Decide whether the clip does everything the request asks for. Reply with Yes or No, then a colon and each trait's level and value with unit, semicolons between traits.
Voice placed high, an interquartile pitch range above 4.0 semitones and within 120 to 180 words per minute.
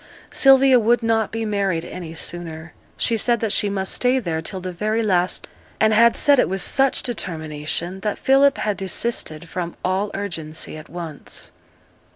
Yes: high, 195 Hz; average, 5.0 semitones; average, 170 wpm